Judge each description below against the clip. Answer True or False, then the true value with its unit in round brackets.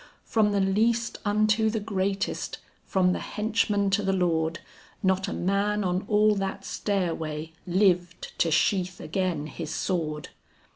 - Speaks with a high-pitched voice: True (195 Hz)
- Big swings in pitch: False (2.8 semitones)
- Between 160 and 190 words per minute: False (140 wpm)